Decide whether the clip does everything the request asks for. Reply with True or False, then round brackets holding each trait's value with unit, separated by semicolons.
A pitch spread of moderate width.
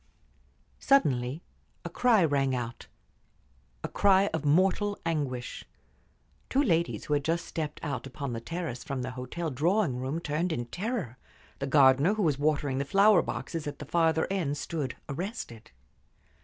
True (4.9 semitones)